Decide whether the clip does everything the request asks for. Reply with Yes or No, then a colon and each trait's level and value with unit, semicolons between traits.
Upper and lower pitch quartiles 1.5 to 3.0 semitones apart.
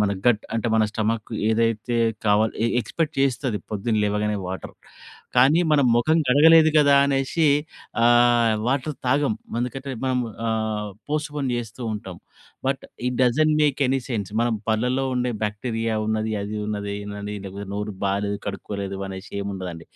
No: average, 4.3 semitones